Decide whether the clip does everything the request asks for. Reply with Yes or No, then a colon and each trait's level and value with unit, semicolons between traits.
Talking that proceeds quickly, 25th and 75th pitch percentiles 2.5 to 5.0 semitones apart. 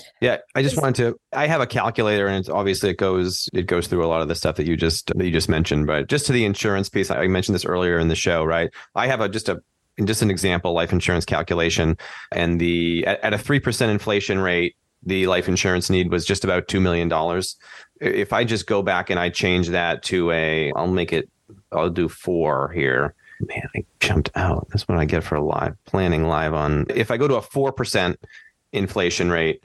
Yes: fast, 225 wpm; average, 3.2 semitones